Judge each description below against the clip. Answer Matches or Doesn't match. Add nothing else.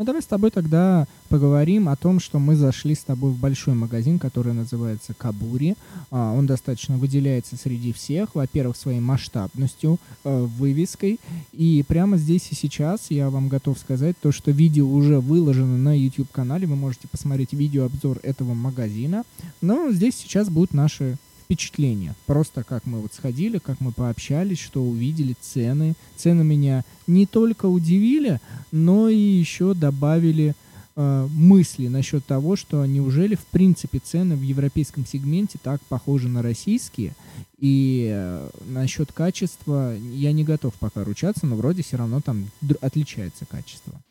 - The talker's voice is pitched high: Doesn't match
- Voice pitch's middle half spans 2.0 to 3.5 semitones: Doesn't match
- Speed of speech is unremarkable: Matches